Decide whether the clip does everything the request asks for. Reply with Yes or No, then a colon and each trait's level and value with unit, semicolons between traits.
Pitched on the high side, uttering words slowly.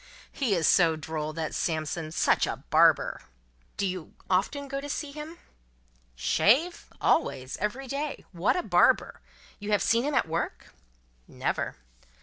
No: high, 195 Hz; average, 150 wpm